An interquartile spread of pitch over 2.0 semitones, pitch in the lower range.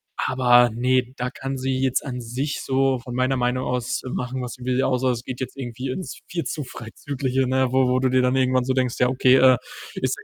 No: narrow, 1.0 semitones; low, 130 Hz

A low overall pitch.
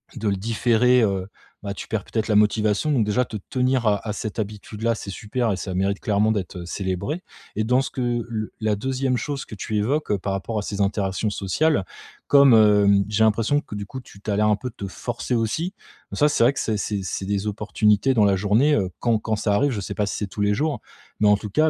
Yes: low, 105 Hz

